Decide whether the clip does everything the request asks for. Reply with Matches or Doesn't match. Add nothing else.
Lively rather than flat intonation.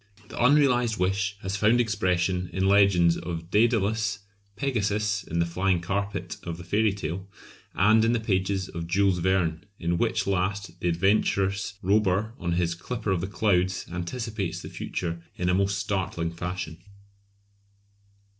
Doesn't match